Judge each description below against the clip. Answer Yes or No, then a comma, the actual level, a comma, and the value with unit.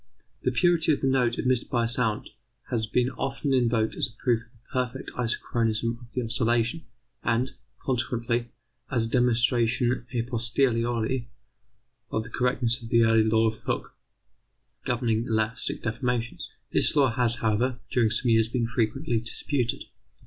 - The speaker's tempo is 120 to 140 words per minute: No, average, 155 wpm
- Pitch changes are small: Yes, narrow, 1.6 semitones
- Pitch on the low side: Yes, low, 120 Hz